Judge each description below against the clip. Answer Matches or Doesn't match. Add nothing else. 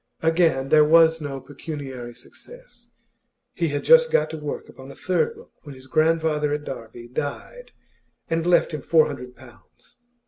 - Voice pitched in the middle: Matches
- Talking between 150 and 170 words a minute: Matches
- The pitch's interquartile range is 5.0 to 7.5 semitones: Doesn't match